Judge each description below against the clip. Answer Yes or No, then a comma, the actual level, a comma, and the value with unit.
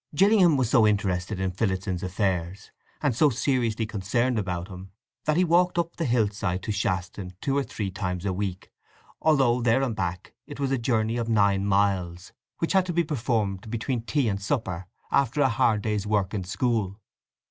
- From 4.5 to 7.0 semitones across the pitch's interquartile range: Yes, average, 5.2 semitones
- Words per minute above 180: Yes, average, 190 wpm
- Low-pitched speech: Yes, low, 110 Hz